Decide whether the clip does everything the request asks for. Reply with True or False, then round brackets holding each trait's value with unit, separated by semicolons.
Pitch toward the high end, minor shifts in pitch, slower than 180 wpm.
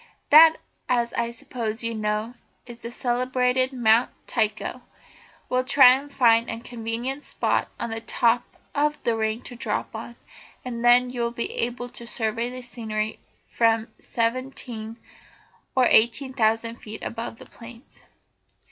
True (235 Hz; 1.8 semitones; 150 wpm)